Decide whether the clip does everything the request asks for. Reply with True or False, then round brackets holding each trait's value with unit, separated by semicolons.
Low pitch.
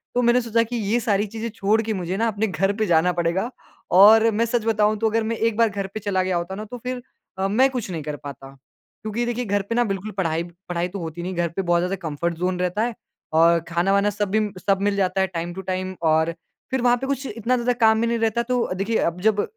False (200 Hz)